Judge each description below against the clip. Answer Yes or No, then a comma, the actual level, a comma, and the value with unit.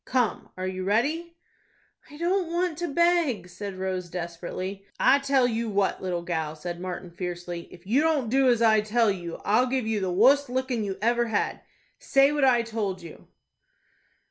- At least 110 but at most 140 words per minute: No, average, 180 wpm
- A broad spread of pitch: Yes, wide, 6.5 semitones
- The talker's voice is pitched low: No, high, 220 Hz